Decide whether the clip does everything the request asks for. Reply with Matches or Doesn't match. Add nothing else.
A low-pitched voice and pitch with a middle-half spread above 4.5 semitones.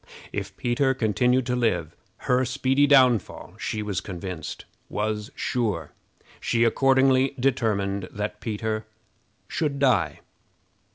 Doesn't match